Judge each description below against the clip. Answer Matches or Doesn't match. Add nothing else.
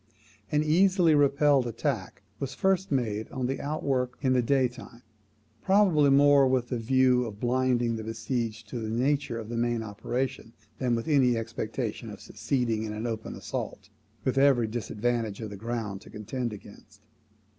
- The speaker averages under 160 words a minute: Doesn't match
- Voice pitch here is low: Matches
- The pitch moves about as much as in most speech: Matches